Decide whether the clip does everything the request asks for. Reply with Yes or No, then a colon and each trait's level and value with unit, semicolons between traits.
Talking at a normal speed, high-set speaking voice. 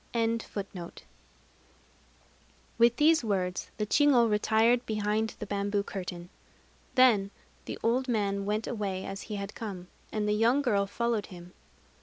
No: slow, 130 wpm; high, 210 Hz